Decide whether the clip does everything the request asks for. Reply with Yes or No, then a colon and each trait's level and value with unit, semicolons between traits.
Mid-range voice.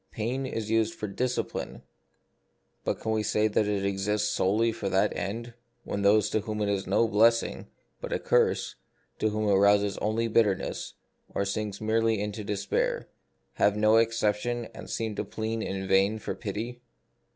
No: low, 105 Hz